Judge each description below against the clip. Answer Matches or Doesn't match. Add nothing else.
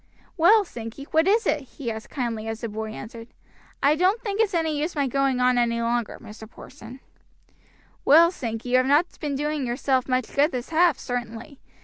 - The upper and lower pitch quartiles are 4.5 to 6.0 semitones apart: Matches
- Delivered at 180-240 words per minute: Matches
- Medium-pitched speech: Doesn't match